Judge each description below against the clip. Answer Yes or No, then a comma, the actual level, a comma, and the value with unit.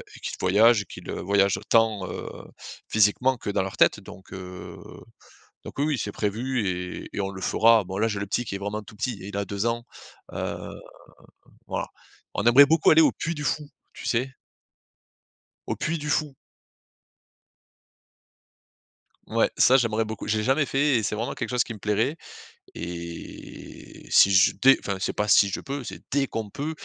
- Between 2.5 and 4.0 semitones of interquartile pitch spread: No, average, 4.8 semitones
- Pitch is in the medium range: No, low, 110 Hz